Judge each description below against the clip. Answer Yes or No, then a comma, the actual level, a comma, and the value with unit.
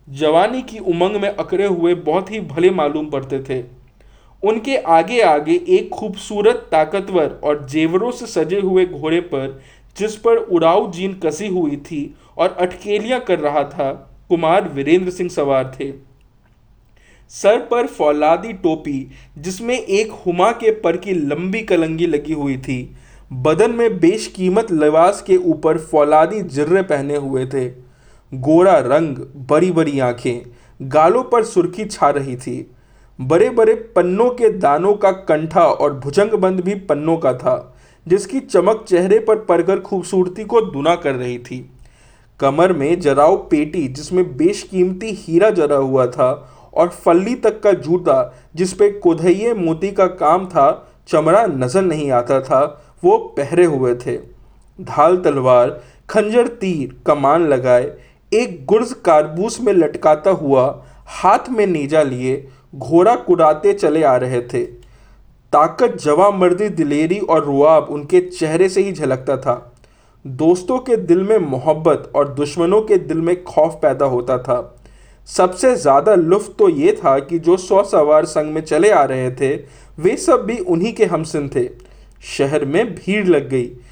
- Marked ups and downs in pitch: Yes, wide, 6.3 semitones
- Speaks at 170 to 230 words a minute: No, average, 150 wpm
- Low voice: No, medium, 170 Hz